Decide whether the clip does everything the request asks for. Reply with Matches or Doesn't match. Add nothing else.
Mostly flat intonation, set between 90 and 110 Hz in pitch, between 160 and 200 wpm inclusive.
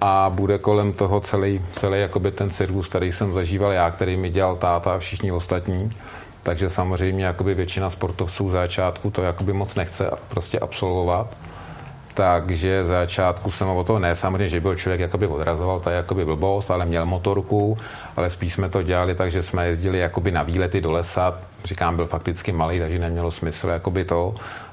Matches